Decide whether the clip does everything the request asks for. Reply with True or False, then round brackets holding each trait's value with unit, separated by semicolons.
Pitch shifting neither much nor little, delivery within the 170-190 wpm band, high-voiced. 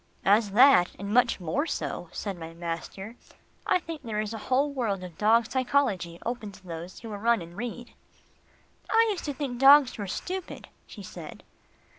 False (5.7 semitones; 180 wpm; 225 Hz)